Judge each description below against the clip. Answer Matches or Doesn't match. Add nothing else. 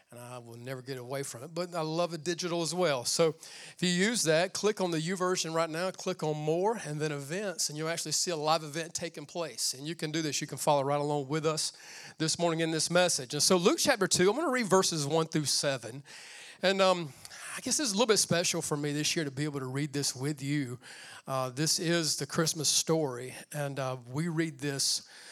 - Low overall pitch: Doesn't match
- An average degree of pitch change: Matches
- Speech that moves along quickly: Matches